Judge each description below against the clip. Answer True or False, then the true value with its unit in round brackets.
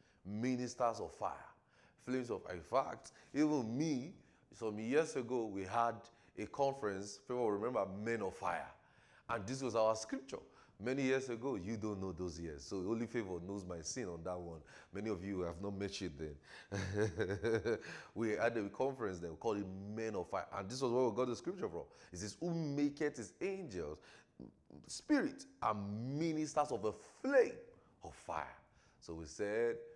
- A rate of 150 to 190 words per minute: True (180 wpm)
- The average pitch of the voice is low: True (115 Hz)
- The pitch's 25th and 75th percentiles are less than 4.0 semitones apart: False (4.9 semitones)